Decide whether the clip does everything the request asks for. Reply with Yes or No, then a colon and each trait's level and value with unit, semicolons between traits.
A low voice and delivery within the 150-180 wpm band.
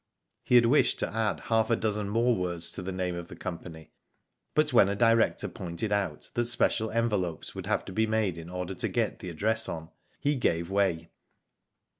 No: low, 100 Hz; average, 200 wpm